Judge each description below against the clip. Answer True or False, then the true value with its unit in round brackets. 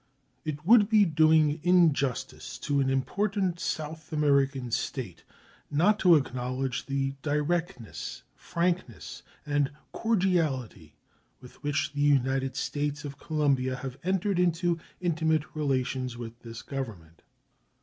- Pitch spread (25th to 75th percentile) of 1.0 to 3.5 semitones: False (4.2 semitones)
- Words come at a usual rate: False (115 wpm)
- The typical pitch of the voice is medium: True (145 Hz)